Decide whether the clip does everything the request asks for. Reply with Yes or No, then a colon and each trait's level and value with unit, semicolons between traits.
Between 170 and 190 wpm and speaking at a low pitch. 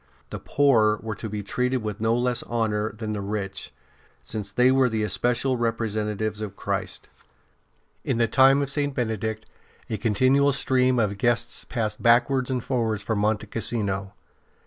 No: average, 160 wpm; low, 115 Hz